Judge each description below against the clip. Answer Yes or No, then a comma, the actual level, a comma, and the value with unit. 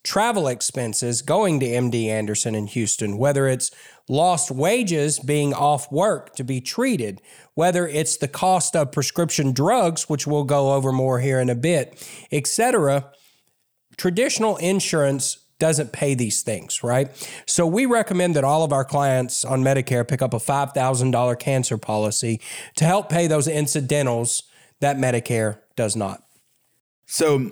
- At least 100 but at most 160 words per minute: Yes, average, 150 wpm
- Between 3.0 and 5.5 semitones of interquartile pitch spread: Yes, average, 4.1 semitones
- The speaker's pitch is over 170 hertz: No, medium, 140 Hz